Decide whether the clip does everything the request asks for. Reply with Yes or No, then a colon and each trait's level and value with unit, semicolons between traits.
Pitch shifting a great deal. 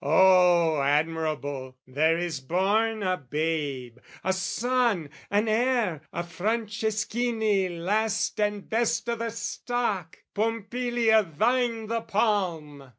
Yes: wide, 5.7 semitones